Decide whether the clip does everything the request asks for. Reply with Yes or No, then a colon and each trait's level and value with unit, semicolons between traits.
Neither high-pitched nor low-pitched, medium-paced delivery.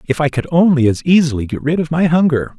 No: medium, 150 Hz; fast, 255 wpm